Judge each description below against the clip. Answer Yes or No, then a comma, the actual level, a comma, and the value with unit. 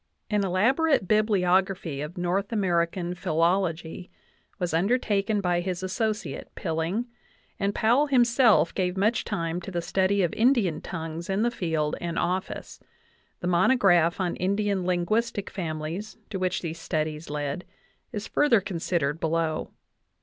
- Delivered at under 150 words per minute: Yes, slow, 135 wpm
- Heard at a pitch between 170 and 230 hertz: Yes, medium, 185 Hz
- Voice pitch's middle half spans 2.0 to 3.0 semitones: No, average, 3.6 semitones